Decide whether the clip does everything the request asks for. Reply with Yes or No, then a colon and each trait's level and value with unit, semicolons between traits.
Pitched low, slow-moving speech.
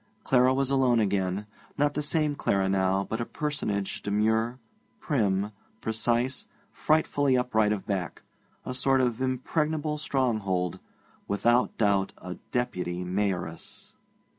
Yes: low, 115 Hz; slow, 120 wpm